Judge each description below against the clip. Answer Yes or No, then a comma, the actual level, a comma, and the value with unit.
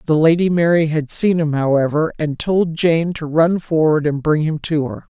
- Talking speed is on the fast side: Yes, fast, 210 wpm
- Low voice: No, medium, 160 Hz